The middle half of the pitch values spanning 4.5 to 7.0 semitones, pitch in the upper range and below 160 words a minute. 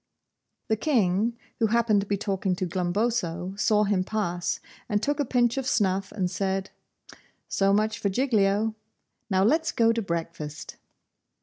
No: average, 3.3 semitones; high, 205 Hz; average, 150 wpm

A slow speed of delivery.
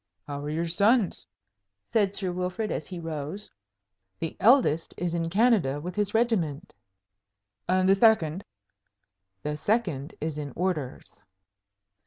Yes: slow, 130 wpm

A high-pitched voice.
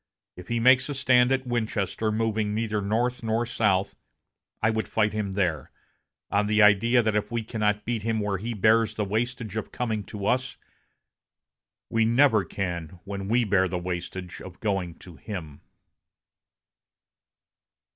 No: low, 110 Hz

